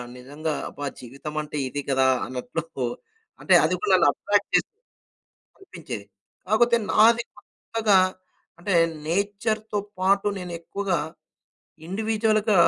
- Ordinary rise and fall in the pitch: No, wide, 6.2 semitones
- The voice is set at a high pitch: Yes, high, 195 Hz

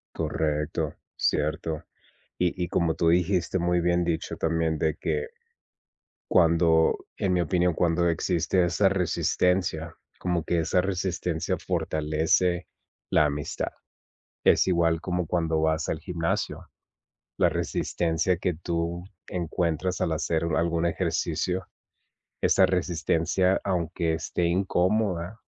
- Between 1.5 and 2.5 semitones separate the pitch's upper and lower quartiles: Yes, narrow, 1.9 semitones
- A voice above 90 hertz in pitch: No, very low, 85 Hz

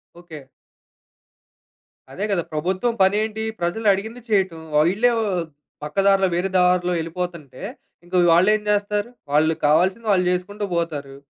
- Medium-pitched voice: Yes, medium, 180 Hz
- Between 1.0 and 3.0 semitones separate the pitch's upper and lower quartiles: No, average, 3.6 semitones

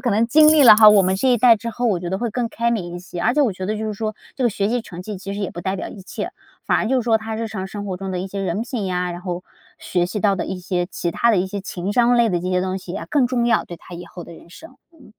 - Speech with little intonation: No, average, 4.3 semitones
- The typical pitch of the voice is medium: No, high, 200 Hz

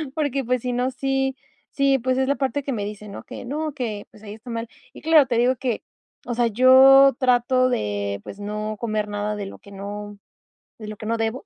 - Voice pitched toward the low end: No, high, 240 Hz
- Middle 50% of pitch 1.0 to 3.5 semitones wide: No, average, 4.0 semitones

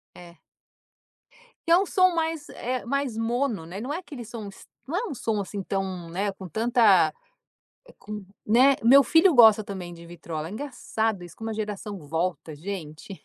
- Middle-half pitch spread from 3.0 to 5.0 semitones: No, wide, 5.6 semitones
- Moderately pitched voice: No, high, 215 Hz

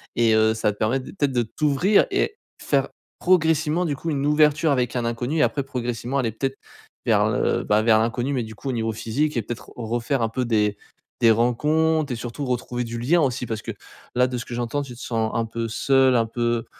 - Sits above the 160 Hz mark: No, low, 125 Hz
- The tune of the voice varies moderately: Yes, average, 3.7 semitones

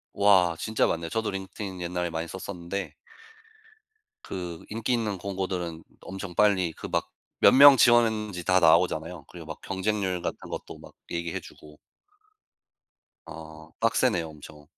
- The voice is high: No, very low, 90 Hz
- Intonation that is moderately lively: Yes, average, 3.6 semitones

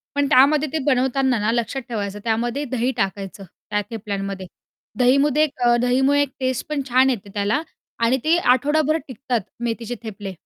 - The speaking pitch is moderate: No, high, 245 Hz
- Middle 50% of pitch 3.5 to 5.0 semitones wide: Yes, average, 4.3 semitones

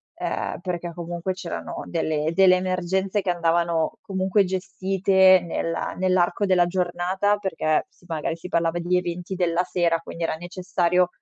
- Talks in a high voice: No, medium, 180 Hz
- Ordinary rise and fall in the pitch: No, narrow, 1.8 semitones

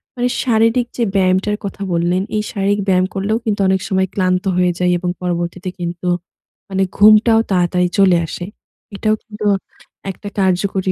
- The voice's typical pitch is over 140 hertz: Yes, high, 190 Hz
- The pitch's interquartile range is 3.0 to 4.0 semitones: No, narrow, 2.5 semitones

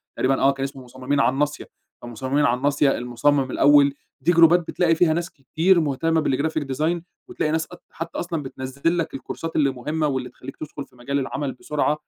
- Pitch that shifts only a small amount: No, average, 3.2 semitones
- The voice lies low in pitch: No, medium, 145 Hz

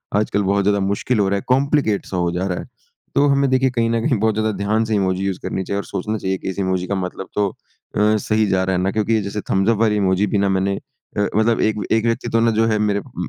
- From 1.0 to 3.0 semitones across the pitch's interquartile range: Yes, narrow, 2.5 semitones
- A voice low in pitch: Yes, low, 105 Hz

